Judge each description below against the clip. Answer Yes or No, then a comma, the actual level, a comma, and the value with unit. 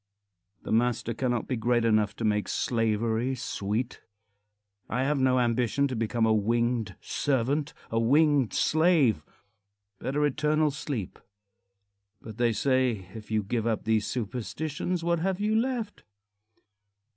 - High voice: No, low, 120 Hz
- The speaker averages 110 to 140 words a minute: Yes, slow, 135 wpm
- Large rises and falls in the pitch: No, average, 4.4 semitones